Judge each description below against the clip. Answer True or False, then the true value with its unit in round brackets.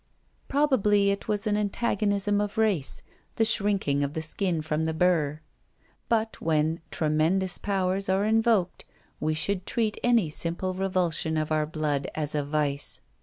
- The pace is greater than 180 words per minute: False (150 wpm)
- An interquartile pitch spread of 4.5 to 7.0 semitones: True (4.9 semitones)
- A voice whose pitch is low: False (185 Hz)